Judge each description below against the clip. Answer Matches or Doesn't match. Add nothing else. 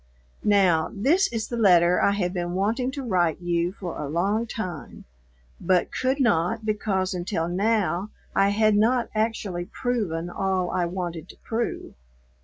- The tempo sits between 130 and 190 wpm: Matches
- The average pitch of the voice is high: Matches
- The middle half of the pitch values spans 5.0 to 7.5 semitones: Doesn't match